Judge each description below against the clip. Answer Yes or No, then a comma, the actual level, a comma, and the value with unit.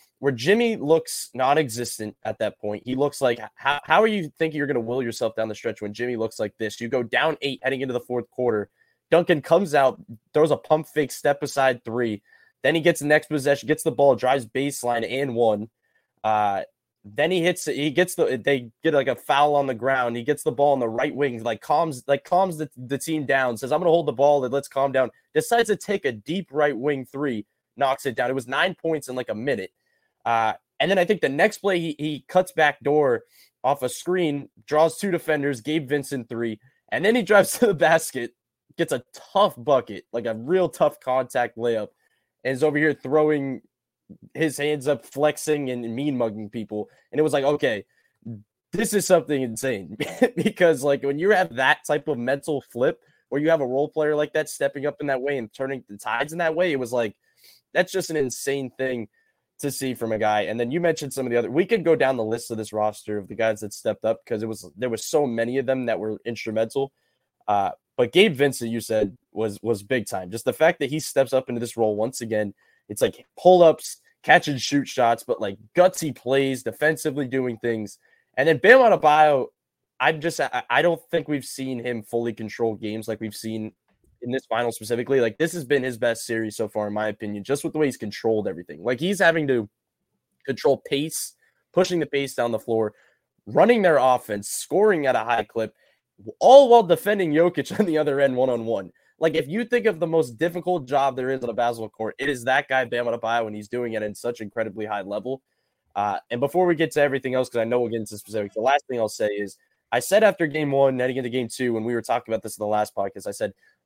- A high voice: No, low, 135 Hz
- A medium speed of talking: No, fast, 235 wpm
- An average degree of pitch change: Yes, average, 5.0 semitones